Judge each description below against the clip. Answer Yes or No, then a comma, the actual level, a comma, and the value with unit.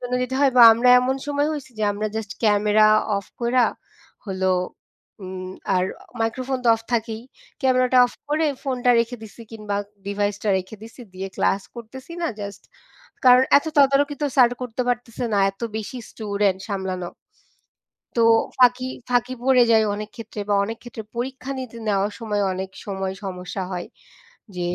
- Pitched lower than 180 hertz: No, high, 225 Hz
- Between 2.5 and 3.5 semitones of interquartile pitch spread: No, average, 3.9 semitones